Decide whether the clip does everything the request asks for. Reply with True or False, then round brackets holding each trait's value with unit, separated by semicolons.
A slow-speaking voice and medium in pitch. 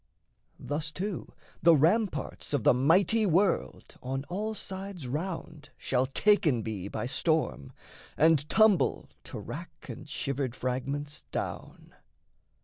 True (120 wpm; 155 Hz)